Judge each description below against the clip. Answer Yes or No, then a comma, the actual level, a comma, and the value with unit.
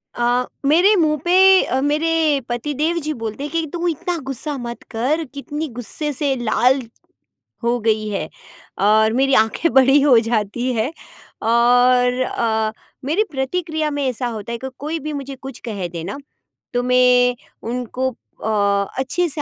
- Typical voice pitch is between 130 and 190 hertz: No, very high, 255 Hz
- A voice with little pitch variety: No, average, 4.2 semitones